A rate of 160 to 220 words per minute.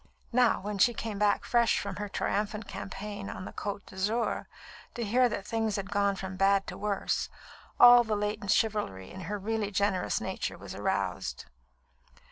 Yes: average, 170 wpm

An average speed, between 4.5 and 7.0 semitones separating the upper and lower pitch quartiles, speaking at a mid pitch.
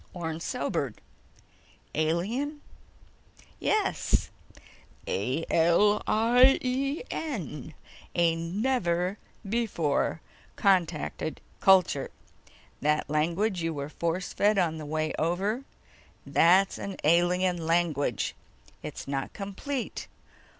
No: slow, 90 wpm; average, 4.8 semitones; medium, 175 Hz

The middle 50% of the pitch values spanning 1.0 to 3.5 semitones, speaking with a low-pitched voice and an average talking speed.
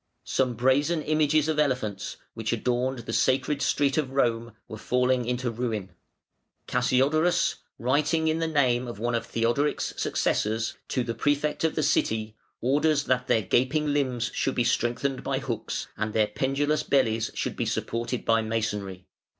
No: average, 4.0 semitones; low, 125 Hz; average, 160 wpm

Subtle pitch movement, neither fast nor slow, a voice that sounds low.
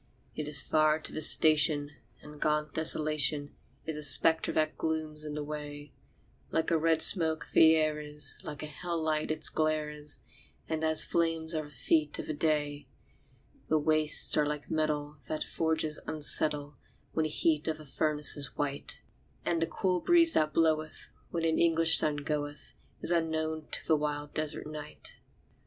No: narrow, 1.2 semitones; average, 175 wpm; medium, 155 Hz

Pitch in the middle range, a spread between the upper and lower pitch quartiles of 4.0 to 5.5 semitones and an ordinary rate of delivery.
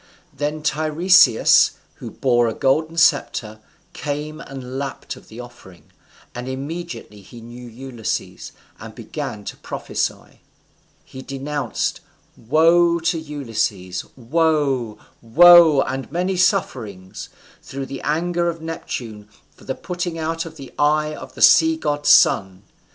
No: medium, 145 Hz; average, 5.2 semitones; slow, 130 wpm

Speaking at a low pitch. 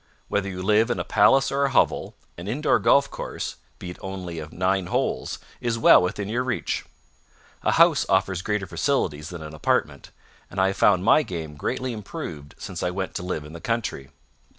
Yes: very low, 95 Hz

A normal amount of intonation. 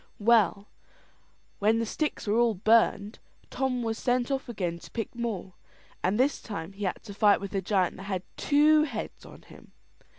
Yes: average, 3.5 semitones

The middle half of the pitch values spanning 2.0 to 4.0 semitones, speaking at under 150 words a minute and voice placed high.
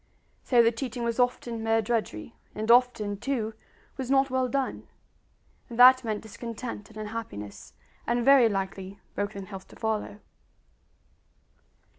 Yes: average, 3.0 semitones; slow, 135 wpm; high, 230 Hz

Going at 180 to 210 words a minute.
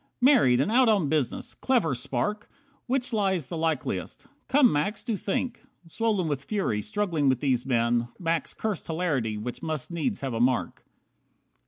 No: average, 160 wpm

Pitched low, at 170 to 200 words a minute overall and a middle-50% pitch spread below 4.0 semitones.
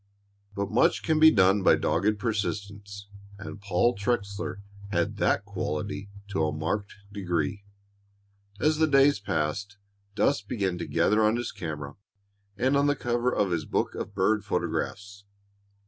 No: low, 100 Hz; average, 145 wpm; average, 3.4 semitones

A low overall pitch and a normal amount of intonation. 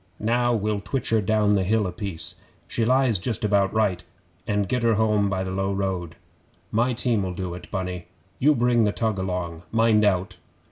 Yes: low, 105 Hz; average, 3.1 semitones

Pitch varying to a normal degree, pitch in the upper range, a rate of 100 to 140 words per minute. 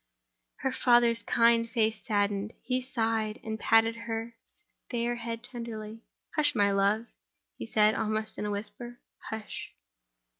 No: narrow, 1.6 semitones; high, 225 Hz; slow, 135 wpm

